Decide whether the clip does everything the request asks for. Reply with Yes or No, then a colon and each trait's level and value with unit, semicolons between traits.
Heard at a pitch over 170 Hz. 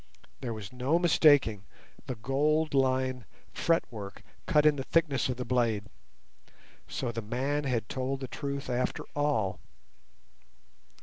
No: low, 130 Hz